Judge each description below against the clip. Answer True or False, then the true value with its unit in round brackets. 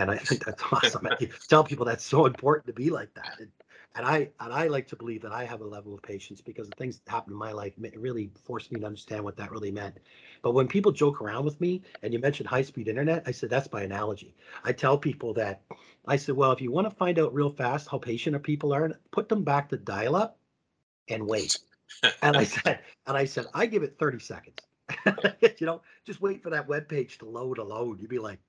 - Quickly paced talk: True (250 wpm)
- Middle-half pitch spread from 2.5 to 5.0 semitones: False (5.5 semitones)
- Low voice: True (130 Hz)